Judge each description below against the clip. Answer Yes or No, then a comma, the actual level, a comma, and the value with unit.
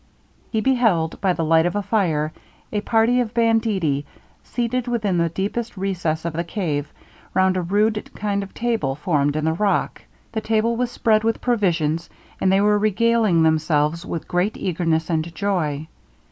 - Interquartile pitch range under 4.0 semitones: No, average, 5.3 semitones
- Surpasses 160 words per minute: Yes, average, 170 wpm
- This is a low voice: No, high, 190 Hz